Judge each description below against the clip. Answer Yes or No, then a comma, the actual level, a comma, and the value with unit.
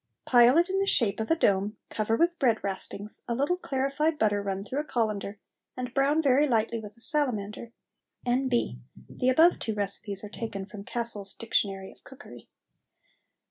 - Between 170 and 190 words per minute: Yes, average, 175 wpm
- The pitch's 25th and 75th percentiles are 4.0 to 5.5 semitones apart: Yes, average, 5.0 semitones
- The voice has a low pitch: No, high, 235 Hz